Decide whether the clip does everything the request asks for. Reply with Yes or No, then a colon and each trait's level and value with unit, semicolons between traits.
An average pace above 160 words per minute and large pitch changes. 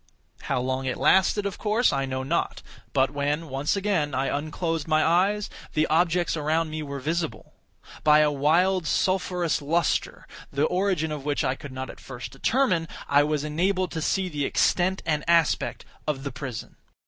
No: average, 175 wpm; average, 3.9 semitones